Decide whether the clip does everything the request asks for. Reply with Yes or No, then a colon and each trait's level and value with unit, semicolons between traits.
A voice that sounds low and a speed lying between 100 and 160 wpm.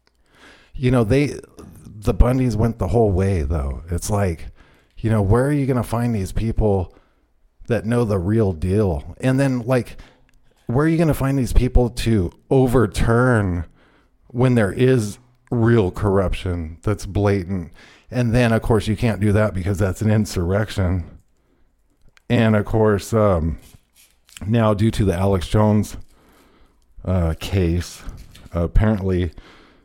Yes: low, 105 Hz; average, 145 wpm